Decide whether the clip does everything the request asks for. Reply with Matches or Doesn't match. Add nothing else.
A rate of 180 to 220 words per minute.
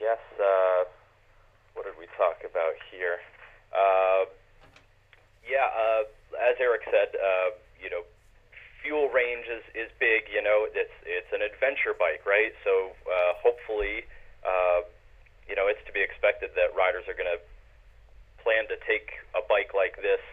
Doesn't match